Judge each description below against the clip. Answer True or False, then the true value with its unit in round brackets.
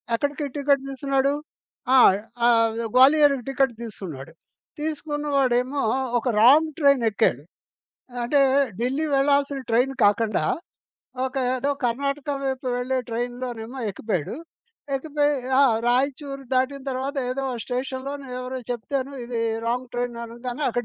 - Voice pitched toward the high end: True (260 Hz)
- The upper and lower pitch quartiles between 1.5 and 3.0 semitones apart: True (2.6 semitones)